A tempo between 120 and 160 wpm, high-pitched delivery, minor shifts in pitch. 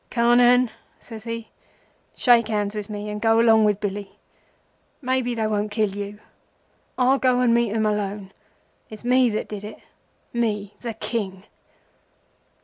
Yes: average, 145 wpm; high, 220 Hz; narrow, 2.3 semitones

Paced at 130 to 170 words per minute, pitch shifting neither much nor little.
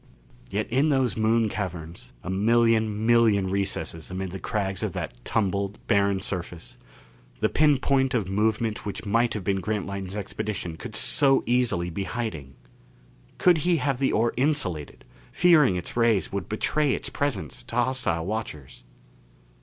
Yes: average, 150 wpm; average, 4.2 semitones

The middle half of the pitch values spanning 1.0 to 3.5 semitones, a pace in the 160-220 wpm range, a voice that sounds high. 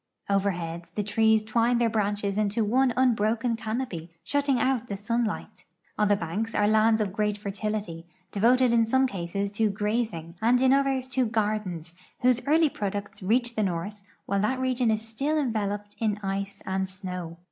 Yes: average, 3.2 semitones; average, 170 wpm; high, 215 Hz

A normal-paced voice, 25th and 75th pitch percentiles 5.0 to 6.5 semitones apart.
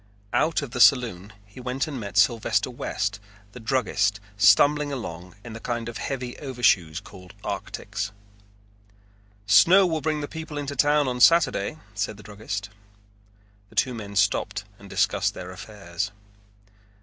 Yes: average, 150 wpm; wide, 5.4 semitones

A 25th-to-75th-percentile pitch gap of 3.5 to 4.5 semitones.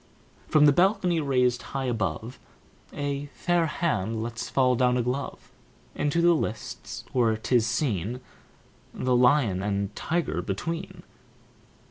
No: average, 5.2 semitones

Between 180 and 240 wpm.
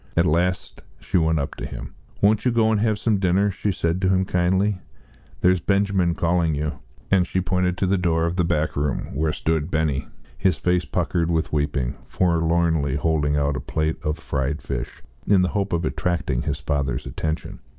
Yes: average, 190 wpm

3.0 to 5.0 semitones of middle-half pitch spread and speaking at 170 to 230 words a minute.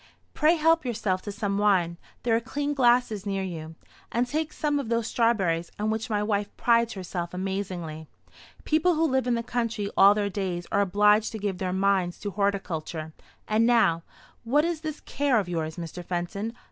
Yes: average, 4.6 semitones; average, 185 wpm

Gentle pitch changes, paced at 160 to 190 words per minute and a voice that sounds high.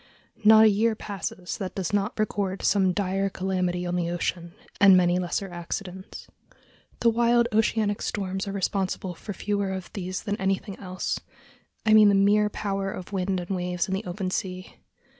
Yes: narrow, 2.0 semitones; average, 170 wpm; high, 195 Hz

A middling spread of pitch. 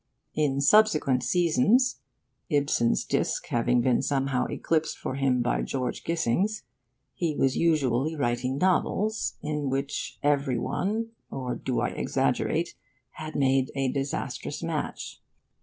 Yes: average, 3.9 semitones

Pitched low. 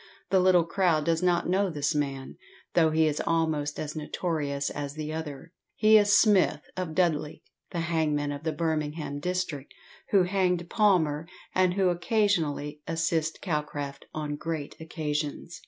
No: medium, 160 Hz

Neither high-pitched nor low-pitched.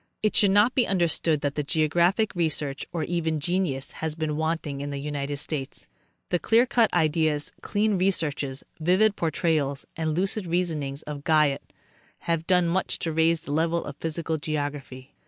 Yes: medium, 160 Hz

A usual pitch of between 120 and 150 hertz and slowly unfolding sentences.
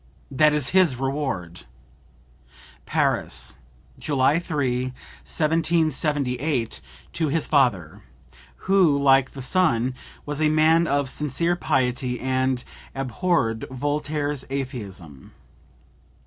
Yes: medium, 140 Hz; slow, 90 wpm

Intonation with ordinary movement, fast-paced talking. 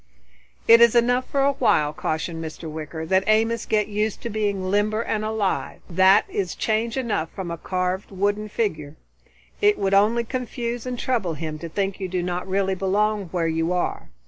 No: average, 4.0 semitones; average, 185 wpm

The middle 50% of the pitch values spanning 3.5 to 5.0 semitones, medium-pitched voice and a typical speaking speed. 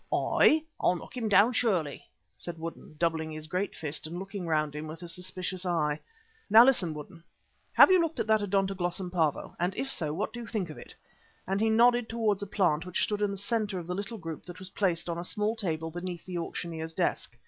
No: average, 4.1 semitones; medium, 180 Hz; fast, 225 wpm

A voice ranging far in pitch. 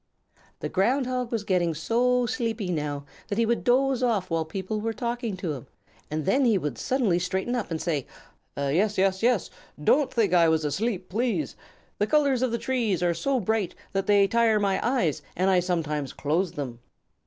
Yes: wide, 5.8 semitones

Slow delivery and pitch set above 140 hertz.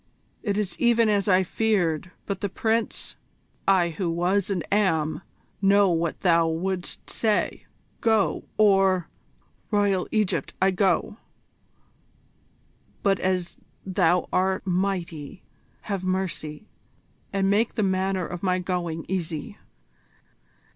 Yes: slow, 120 wpm; high, 190 Hz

